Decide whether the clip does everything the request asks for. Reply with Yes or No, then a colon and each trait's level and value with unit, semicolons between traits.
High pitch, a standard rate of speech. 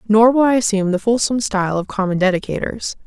Yes: high, 210 Hz; average, 195 wpm